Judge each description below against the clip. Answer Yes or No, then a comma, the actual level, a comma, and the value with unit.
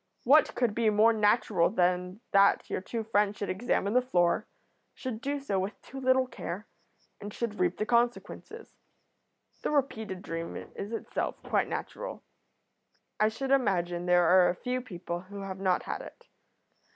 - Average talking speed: Yes, average, 160 wpm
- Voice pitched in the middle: No, high, 210 Hz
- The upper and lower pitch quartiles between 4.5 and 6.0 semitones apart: Yes, average, 4.8 semitones